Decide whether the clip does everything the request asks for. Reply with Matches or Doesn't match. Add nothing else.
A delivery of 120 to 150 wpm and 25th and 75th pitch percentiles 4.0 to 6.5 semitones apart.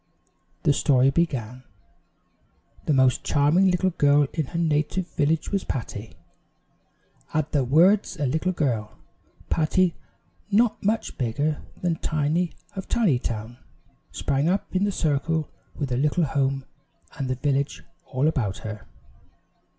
Matches